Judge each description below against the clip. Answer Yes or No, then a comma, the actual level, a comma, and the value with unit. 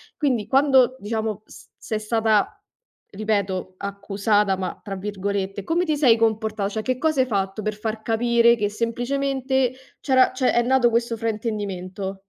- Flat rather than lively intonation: No, average, 3.5 semitones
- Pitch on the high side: Yes, high, 220 Hz